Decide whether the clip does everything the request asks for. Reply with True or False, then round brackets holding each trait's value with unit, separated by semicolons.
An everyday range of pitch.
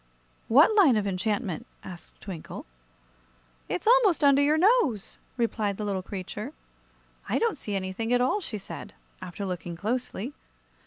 False (6.9 semitones)